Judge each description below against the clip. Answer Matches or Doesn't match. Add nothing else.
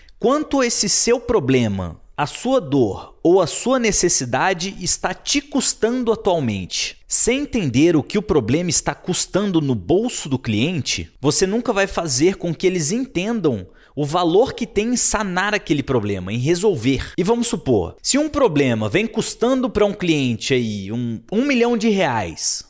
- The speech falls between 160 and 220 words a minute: Matches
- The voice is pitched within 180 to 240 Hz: Matches